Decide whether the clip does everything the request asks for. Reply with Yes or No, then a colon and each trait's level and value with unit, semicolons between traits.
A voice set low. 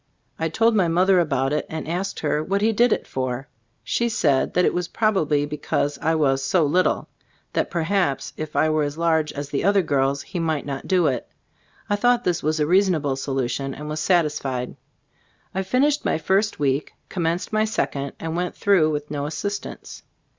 No: medium, 160 Hz